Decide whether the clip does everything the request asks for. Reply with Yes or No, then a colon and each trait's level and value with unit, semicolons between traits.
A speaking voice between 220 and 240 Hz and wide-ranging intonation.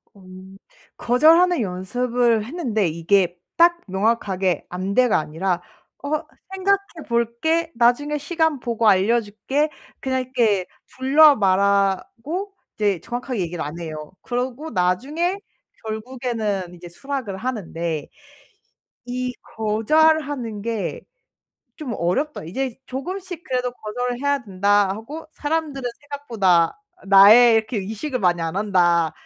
Yes: high, 230 Hz; wide, 6.2 semitones